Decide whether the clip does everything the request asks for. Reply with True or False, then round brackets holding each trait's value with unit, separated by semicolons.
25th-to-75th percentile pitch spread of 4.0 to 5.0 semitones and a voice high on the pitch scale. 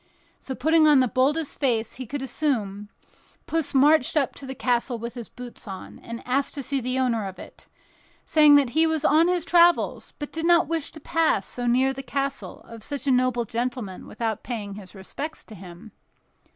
True (4.3 semitones; 260 Hz)